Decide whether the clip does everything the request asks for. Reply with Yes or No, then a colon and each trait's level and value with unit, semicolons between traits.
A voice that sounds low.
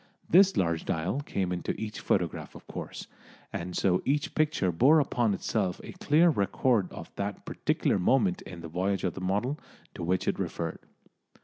Yes: low, 100 Hz